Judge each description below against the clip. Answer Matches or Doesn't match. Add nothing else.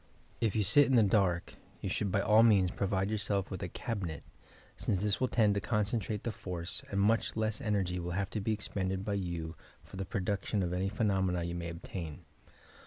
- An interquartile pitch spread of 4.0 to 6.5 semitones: Doesn't match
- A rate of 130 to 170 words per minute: Doesn't match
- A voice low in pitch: Matches